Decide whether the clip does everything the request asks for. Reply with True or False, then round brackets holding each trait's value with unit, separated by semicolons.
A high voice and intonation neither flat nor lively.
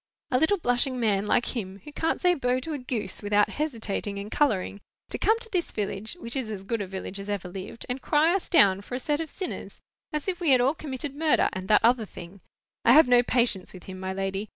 False (240 Hz; 6.7 semitones)